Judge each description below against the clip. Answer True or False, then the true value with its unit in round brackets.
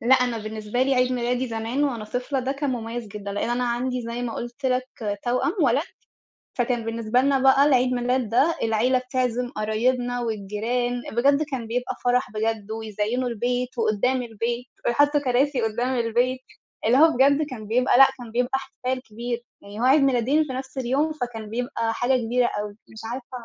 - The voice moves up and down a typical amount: False (2.3 semitones)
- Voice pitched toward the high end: True (245 Hz)